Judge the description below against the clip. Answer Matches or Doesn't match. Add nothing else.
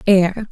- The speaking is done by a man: Doesn't match